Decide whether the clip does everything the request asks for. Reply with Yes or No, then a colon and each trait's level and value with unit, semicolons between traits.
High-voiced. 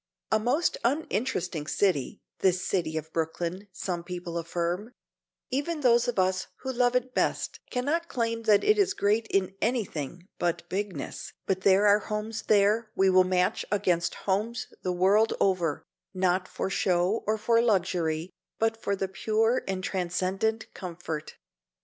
Yes: high, 195 Hz